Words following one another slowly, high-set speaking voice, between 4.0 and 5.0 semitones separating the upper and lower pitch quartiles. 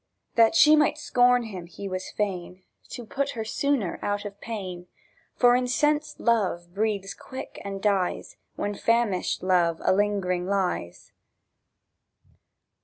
Yes: slow, 130 wpm; high, 205 Hz; average, 4.7 semitones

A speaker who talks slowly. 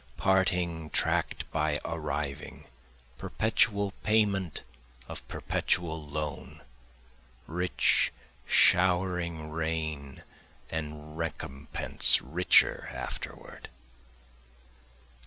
Yes: slow, 65 wpm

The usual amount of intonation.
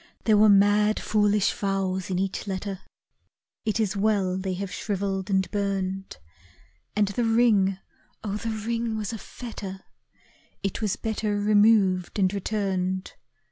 No: narrow, 1.9 semitones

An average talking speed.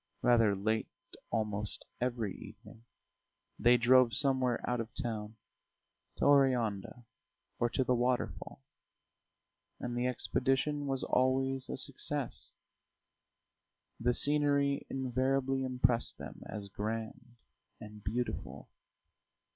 No: slow, 100 wpm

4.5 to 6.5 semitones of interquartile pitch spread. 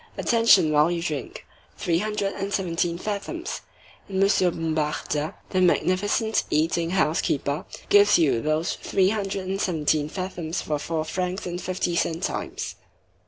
No: average, 3.8 semitones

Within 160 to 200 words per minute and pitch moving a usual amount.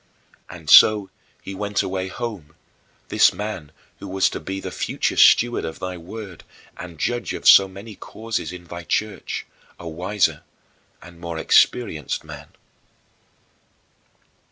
No: slow, 135 wpm; average, 3.6 semitones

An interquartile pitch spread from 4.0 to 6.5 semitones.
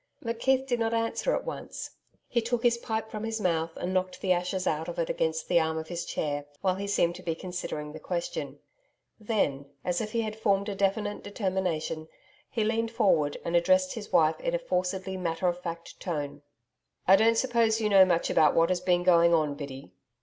Yes: average, 5.1 semitones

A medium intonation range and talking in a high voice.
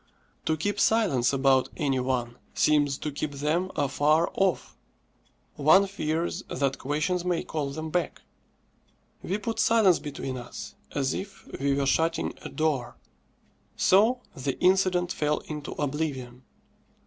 No: average, 4.5 semitones; medium, 150 Hz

